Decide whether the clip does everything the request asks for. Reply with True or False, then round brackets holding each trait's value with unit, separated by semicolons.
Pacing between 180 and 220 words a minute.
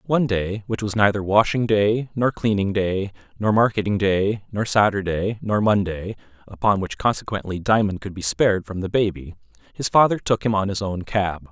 False (170 wpm)